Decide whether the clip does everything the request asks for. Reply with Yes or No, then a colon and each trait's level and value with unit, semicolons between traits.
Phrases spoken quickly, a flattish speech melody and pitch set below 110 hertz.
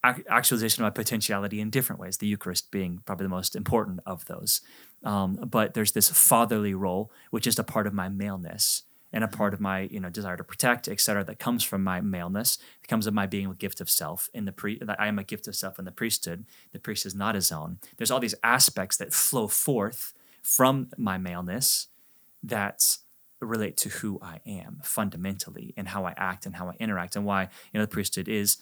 Yes: fast, 220 wpm; narrow, 2.0 semitones; low, 100 Hz